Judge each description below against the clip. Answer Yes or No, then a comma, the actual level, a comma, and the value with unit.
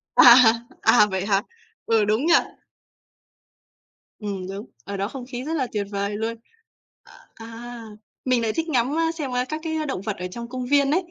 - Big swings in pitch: No, average, 4.8 semitones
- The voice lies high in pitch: Yes, high, 235 Hz